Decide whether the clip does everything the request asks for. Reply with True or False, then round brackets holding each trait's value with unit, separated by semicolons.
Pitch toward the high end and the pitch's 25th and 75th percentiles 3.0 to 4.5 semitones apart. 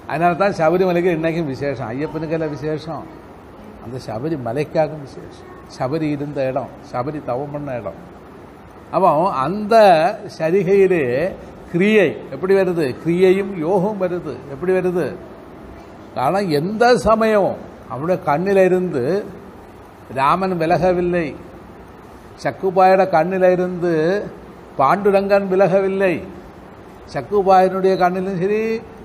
False (180 Hz; 3.9 semitones)